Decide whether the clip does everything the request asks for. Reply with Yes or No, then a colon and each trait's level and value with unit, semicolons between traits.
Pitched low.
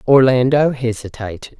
Yes: low, 125 Hz